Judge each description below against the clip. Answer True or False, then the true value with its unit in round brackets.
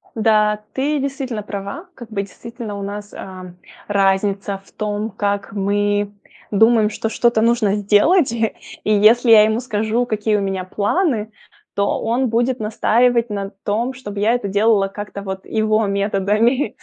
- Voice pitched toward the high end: True (210 Hz)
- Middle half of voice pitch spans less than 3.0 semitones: True (2.5 semitones)